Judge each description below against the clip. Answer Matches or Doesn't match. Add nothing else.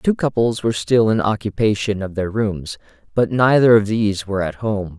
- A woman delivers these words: Doesn't match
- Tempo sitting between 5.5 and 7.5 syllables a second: Doesn't match